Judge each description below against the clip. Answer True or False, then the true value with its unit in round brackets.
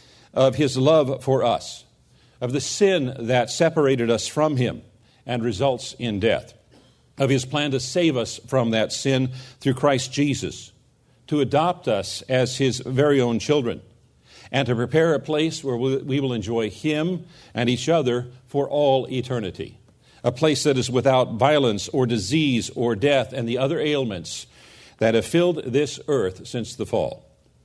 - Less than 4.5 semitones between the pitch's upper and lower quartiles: True (3.1 semitones)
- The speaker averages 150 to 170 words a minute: True (165 wpm)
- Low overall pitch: True (130 Hz)